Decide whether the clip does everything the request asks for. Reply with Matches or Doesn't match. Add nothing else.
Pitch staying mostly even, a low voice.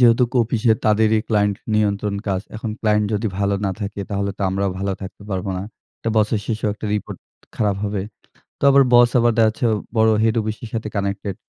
Matches